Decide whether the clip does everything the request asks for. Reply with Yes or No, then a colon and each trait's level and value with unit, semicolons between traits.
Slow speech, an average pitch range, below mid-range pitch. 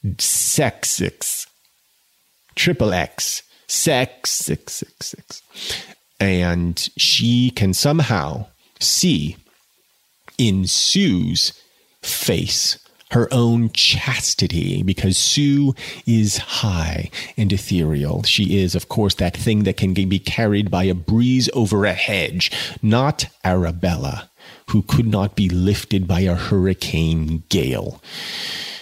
Yes: slow, 110 wpm; average, 4.1 semitones; low, 100 Hz